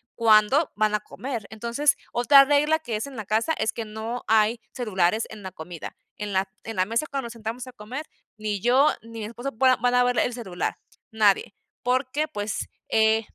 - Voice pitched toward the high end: Yes, high, 225 Hz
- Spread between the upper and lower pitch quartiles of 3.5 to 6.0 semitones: No, average, 2.9 semitones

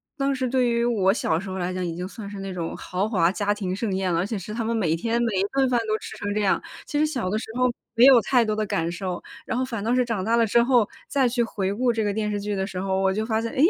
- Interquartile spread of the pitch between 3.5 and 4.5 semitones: Yes, average, 3.8 semitones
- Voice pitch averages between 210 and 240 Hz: Yes, high, 215 Hz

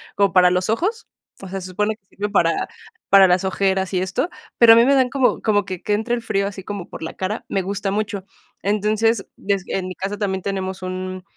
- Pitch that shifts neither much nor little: No, narrow, 2.3 semitones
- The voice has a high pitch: Yes, high, 195 Hz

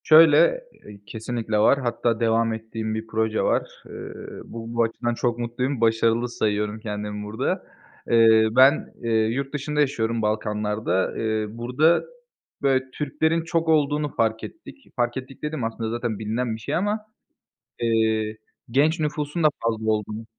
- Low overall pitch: Yes, low, 115 Hz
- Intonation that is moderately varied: Yes, average, 3.7 semitones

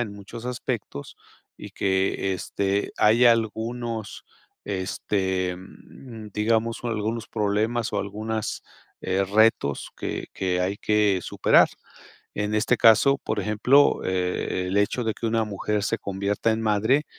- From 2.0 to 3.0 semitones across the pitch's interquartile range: Yes, narrow, 2.6 semitones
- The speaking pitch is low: Yes, low, 105 Hz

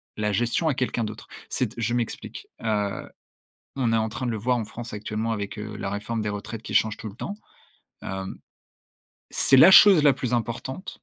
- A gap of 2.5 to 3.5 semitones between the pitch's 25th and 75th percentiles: Yes, average, 2.8 semitones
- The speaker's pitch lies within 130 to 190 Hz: No, low, 115 Hz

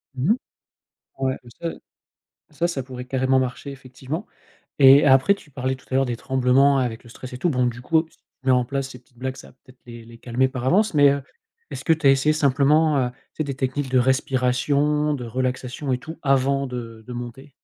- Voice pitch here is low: Yes, low, 130 Hz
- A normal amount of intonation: No, narrow, 2.0 semitones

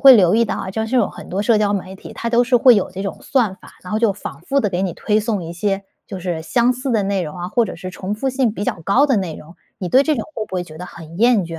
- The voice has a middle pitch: No, high, 200 Hz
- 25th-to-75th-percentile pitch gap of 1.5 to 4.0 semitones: No, average, 4.5 semitones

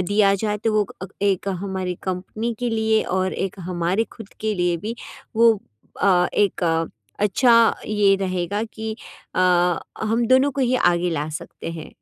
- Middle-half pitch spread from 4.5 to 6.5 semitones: No, average, 3.3 semitones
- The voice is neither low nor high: No, high, 200 Hz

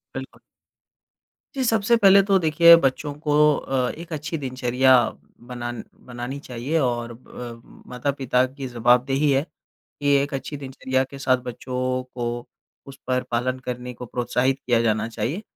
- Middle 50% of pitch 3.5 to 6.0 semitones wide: No, average, 2.7 semitones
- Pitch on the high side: No, low, 130 Hz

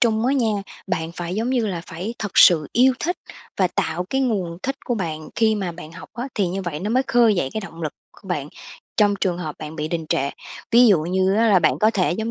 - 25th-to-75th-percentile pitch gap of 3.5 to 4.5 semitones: No, average, 5.0 semitones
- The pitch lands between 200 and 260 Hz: No, high, 190 Hz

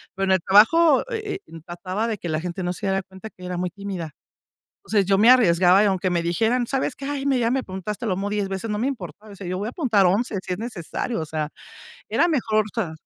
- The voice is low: No, high, 200 Hz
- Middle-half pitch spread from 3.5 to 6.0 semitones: Yes, average, 4.2 semitones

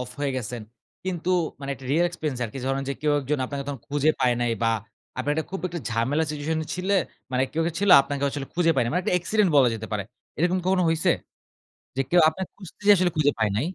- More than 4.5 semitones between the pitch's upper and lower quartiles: Yes, average, 5.0 semitones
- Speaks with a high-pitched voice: No, medium, 145 Hz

